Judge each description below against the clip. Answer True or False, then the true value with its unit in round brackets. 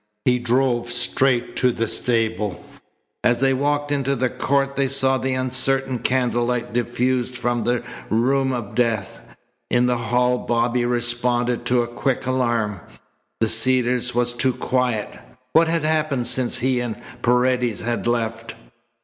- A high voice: False (125 Hz)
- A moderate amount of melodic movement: False (1.5 semitones)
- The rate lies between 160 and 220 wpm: False (145 wpm)